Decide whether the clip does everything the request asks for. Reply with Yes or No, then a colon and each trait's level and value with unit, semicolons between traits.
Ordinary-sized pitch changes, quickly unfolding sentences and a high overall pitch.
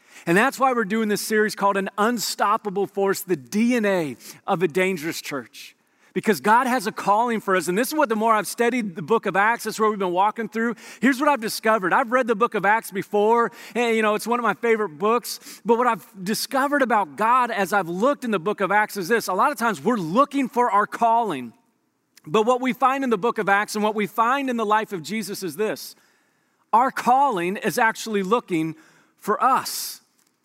Yes: average, 3.1 semitones; fast, 225 wpm; high, 220 Hz